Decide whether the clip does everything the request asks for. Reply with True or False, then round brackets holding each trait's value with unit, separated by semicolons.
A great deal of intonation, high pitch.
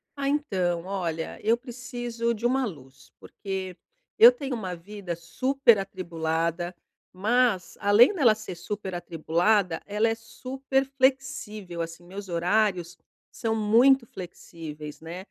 True (5.7 semitones; 205 Hz)